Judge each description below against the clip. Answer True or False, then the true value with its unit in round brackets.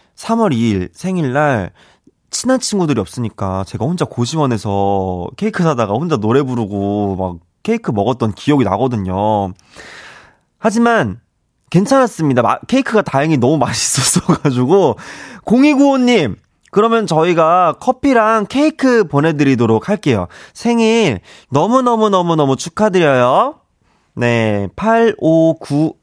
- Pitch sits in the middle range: True (150 Hz)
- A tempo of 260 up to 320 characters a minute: True (270 characters per minute)